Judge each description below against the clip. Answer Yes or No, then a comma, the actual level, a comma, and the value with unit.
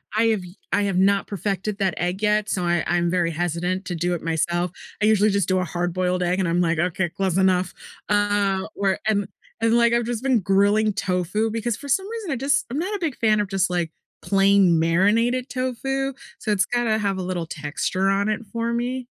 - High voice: Yes, high, 195 Hz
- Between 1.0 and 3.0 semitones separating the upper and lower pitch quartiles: No, average, 4.1 semitones